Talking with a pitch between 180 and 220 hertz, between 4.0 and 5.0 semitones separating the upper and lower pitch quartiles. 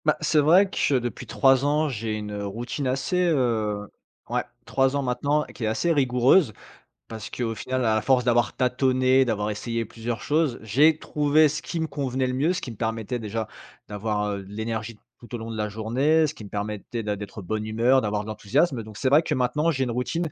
No: low, 120 Hz; average, 4.5 semitones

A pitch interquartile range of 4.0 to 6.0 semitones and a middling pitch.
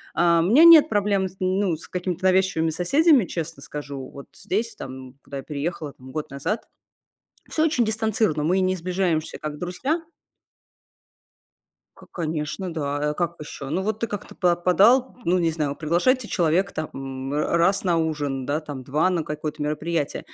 Yes: average, 4.3 semitones; medium, 170 Hz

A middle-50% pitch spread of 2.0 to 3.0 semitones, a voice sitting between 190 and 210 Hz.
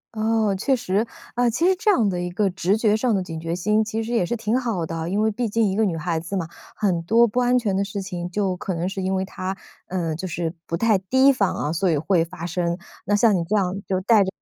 No: average, 3.8 semitones; high, 195 Hz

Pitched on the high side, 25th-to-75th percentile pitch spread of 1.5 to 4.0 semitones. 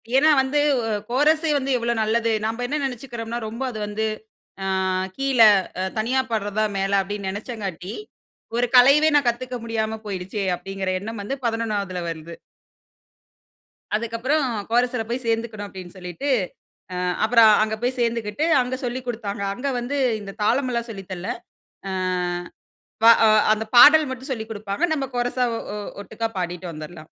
Yes: high, 230 Hz; average, 3.6 semitones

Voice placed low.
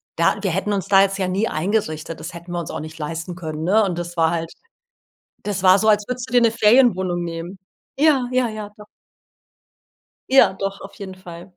No: high, 190 Hz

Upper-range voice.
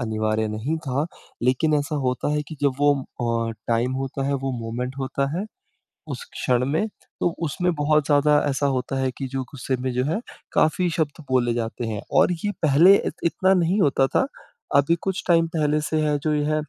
No: medium, 140 Hz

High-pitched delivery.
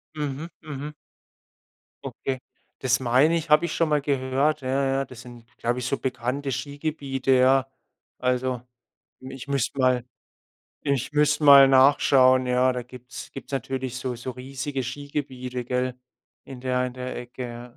No: low, 130 Hz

